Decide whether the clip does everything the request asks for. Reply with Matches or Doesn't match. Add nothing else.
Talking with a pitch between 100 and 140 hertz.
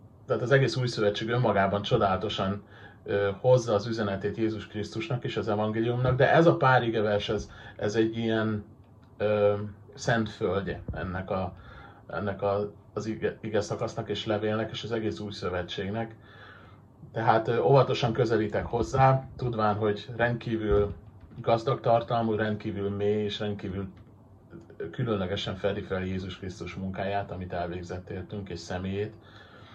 Matches